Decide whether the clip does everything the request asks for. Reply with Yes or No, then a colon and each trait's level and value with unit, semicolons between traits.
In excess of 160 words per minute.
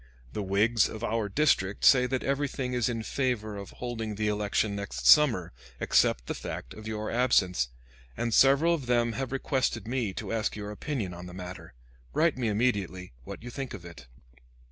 Yes: average, 185 wpm